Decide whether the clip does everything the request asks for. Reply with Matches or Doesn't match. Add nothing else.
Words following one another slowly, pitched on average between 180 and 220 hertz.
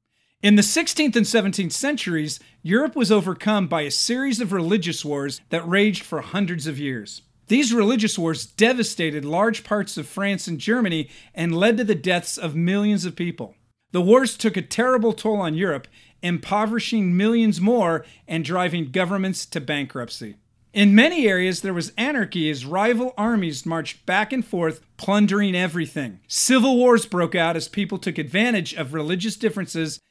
Doesn't match